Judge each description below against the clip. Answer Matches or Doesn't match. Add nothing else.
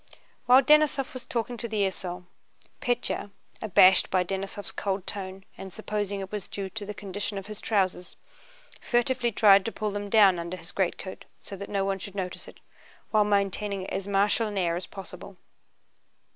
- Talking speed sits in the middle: Matches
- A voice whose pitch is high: Matches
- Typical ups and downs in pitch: Doesn't match